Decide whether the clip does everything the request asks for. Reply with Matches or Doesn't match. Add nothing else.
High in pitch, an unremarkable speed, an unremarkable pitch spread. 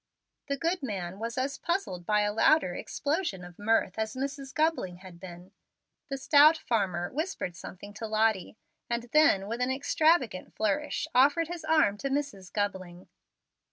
Doesn't match